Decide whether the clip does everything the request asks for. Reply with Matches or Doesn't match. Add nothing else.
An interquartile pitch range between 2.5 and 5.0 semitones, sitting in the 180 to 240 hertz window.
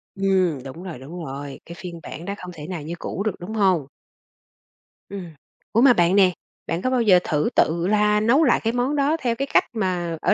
Matches